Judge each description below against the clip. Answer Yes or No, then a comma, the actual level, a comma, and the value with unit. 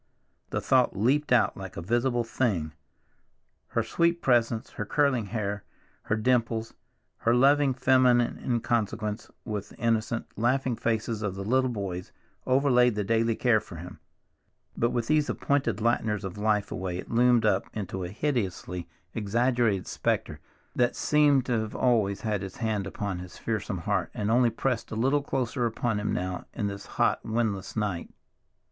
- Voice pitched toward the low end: Yes, low, 115 Hz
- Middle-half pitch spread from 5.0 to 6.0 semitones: No, average, 3.4 semitones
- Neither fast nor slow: Yes, average, 160 wpm